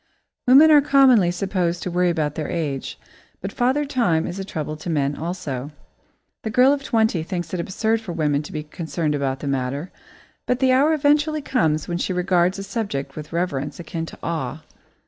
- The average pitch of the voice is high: No, medium, 175 Hz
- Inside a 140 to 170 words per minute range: No, average, 190 wpm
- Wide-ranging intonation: Yes, wide, 6.8 semitones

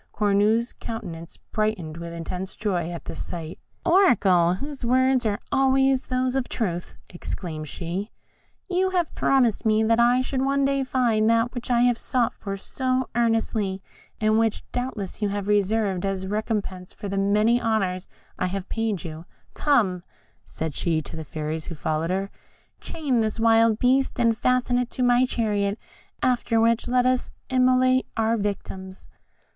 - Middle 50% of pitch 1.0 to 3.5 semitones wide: No, average, 4.8 semitones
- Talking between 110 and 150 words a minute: No, average, 165 wpm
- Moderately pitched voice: No, high, 220 Hz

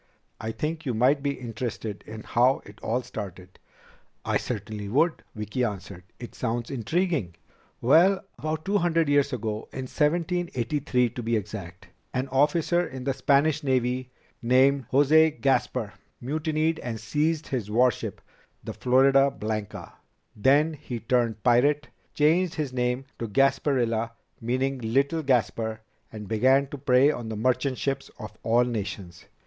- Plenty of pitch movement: No, average, 4.4 semitones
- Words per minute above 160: No, average, 145 wpm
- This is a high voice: No, low, 130 Hz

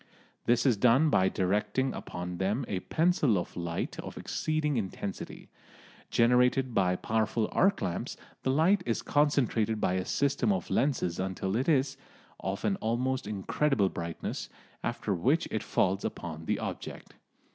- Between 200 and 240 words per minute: No, average, 145 wpm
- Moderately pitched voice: No, low, 115 Hz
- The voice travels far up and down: Yes, wide, 6.3 semitones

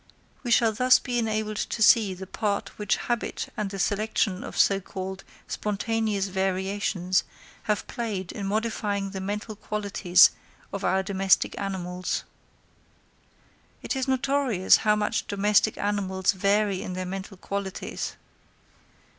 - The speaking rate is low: Yes, slow, 130 wpm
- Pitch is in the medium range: No, high, 200 Hz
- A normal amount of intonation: No, narrow, 2.2 semitones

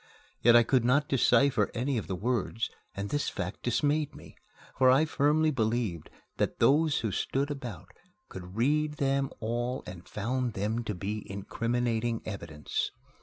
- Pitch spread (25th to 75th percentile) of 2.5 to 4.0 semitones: No, average, 4.7 semitones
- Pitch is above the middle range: No, low, 120 Hz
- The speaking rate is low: No, average, 155 wpm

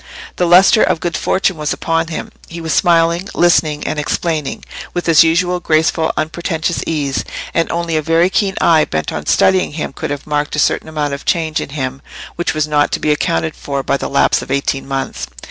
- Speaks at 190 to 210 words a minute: Yes, fast, 205 wpm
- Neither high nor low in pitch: Yes, medium, 160 Hz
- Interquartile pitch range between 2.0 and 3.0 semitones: Yes, narrow, 2.6 semitones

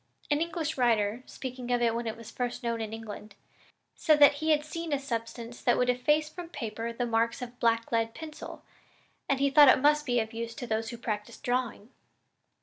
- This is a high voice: Yes, high, 245 Hz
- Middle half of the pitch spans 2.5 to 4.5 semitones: Yes, average, 4.1 semitones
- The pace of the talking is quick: Yes, fast, 215 wpm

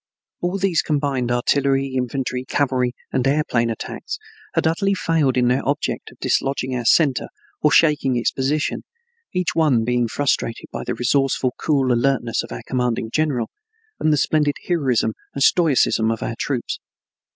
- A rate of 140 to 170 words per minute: Yes, average, 155 wpm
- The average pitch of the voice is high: No, low, 135 Hz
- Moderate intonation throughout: Yes, average, 3.4 semitones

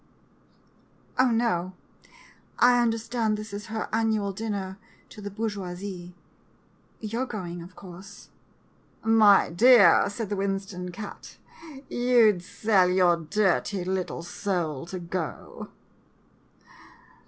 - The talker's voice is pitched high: Yes, high, 200 Hz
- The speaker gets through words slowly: Yes, slow, 125 wpm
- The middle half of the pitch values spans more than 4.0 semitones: No, average, 3.6 semitones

